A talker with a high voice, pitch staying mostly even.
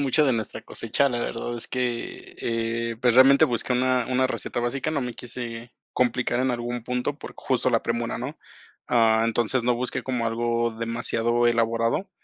No: low, 120 Hz; narrow, 1.5 semitones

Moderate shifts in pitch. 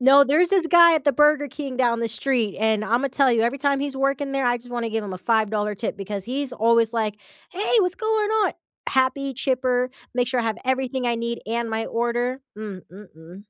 Yes: average, 3.6 semitones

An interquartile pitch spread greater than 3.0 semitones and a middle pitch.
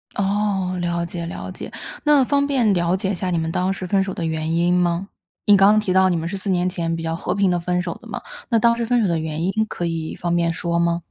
No: narrow, 2.6 semitones; medium, 180 Hz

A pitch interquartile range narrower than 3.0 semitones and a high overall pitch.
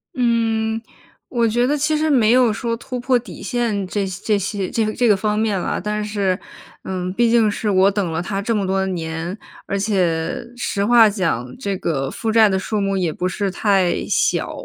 No: average, 3.4 semitones; high, 205 Hz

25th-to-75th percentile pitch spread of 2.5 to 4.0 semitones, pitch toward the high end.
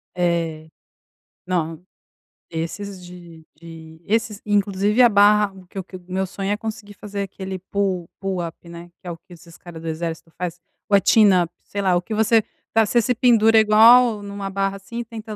Yes: average, 3.4 semitones; high, 195 Hz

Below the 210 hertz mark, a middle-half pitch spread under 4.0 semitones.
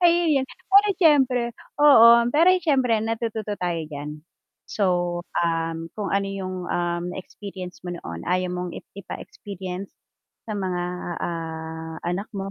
No: medium, 185 Hz; average, 4.7 semitones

